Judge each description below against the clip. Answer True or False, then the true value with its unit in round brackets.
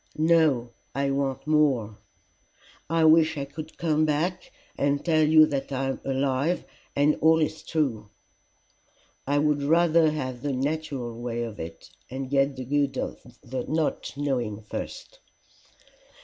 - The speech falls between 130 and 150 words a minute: True (140 wpm)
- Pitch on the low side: False (145 Hz)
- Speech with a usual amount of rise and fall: True (3.0 semitones)